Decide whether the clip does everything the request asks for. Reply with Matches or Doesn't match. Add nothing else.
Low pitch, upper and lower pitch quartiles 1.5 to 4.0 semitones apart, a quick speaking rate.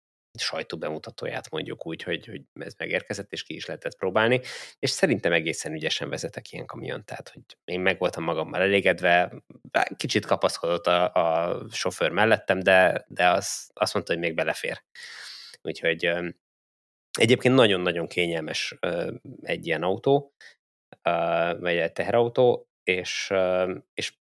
Doesn't match